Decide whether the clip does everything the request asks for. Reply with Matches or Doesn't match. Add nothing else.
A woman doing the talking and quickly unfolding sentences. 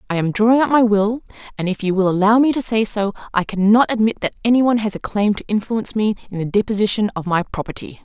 Matches